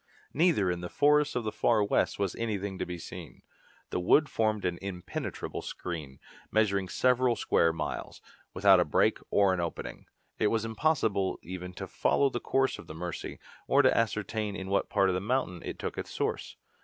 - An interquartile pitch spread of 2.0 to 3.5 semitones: No, average, 4.3 semitones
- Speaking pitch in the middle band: No, low, 100 Hz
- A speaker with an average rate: Yes, average, 190 wpm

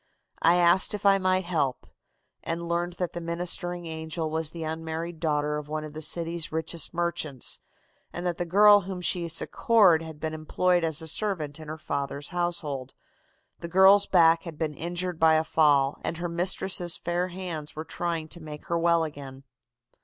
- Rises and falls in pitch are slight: Yes, narrow, 2.0 semitones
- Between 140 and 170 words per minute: No, average, 185 wpm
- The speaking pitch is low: No, medium, 165 Hz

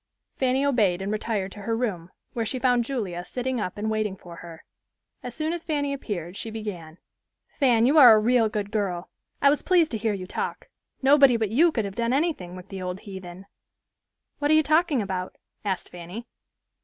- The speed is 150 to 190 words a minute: No, average, 200 wpm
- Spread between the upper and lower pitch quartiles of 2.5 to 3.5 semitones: No, wide, 5.6 semitones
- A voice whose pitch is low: No, high, 220 Hz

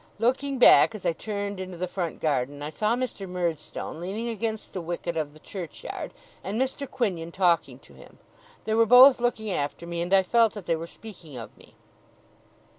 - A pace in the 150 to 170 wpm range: No, average, 190 wpm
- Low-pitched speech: No, high, 190 Hz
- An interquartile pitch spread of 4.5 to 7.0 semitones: Yes, average, 5.0 semitones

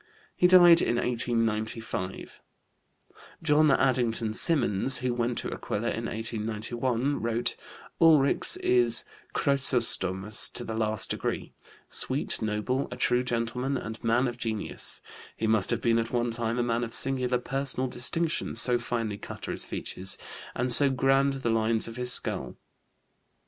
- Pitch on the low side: Yes, low, 120 Hz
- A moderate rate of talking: Yes, average, 145 wpm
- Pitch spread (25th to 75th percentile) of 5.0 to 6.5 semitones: No, narrow, 2.5 semitones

